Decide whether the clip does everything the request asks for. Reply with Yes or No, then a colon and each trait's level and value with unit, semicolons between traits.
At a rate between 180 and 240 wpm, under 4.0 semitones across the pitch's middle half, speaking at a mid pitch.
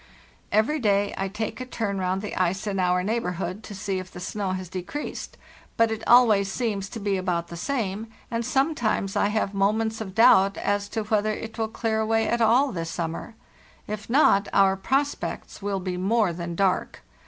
No: average, 200 wpm; average, 2.9 semitones; high, 205 Hz